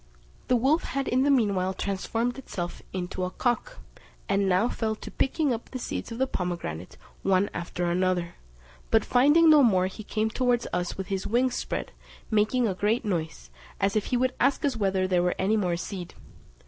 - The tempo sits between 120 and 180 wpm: No, average, 190 wpm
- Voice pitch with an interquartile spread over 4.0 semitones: Yes, average, 5.1 semitones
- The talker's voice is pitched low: No, high, 210 Hz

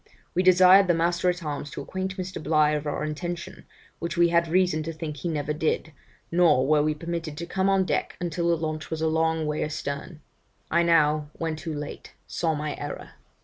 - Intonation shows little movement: Yes, narrow, 2.2 semitones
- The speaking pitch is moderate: Yes, medium, 160 Hz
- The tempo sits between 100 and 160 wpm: No, fast, 205 wpm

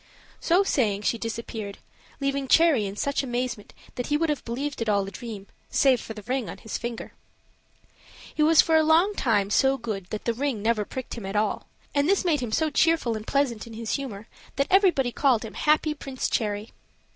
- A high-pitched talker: Yes, high, 245 Hz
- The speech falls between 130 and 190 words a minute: No, fast, 205 wpm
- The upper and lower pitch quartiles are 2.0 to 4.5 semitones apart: No, average, 4.9 semitones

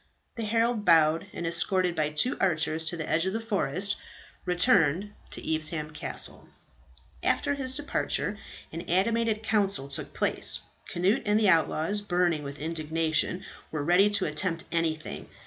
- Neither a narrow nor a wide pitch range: Yes, average, 4.7 semitones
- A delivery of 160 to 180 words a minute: No, average, 145 wpm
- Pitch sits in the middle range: Yes, medium, 175 Hz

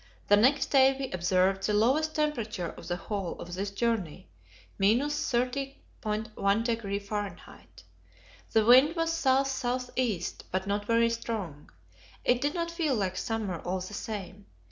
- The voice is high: Yes, high, 225 Hz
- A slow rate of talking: No, average, 145 wpm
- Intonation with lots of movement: No, average, 5.0 semitones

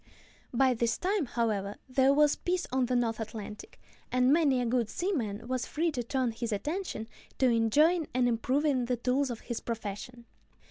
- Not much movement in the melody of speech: No, average, 3.7 semitones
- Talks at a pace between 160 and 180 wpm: Yes, average, 175 wpm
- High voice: Yes, very high, 250 Hz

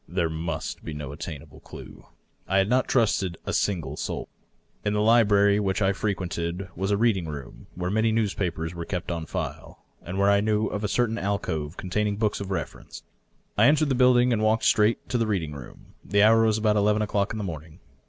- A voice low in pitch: Yes, low, 100 Hz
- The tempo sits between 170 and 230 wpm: Yes, fast, 205 wpm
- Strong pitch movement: No, average, 3.9 semitones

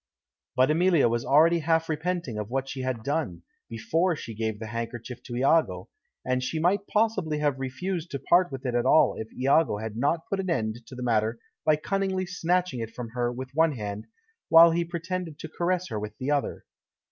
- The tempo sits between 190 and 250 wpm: Yes, fast, 205 wpm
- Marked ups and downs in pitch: Yes, wide, 6.2 semitones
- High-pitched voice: No, medium, 140 Hz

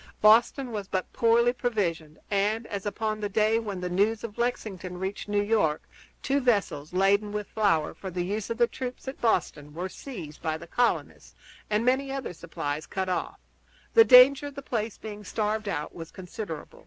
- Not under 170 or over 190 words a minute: Yes, average, 185 wpm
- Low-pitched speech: No, high, 210 Hz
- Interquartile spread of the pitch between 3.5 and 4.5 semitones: Yes, average, 4.2 semitones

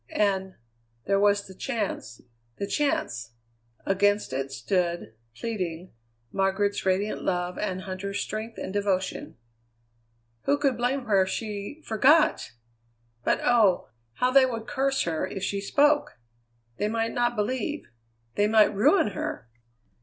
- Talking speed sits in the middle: No, slow, 130 wpm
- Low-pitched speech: No, high, 205 Hz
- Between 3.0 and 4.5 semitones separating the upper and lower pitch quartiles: Yes, average, 4.2 semitones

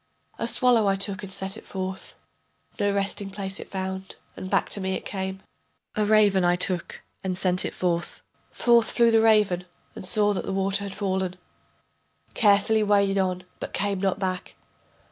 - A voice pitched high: Yes, high, 195 Hz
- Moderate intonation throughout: No, narrow, 1.5 semitones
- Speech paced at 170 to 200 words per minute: Yes, average, 180 wpm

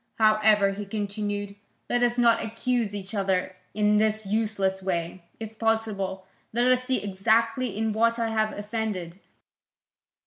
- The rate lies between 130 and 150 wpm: Yes, average, 140 wpm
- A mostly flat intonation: Yes, narrow, 2.3 semitones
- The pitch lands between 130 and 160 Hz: No, high, 215 Hz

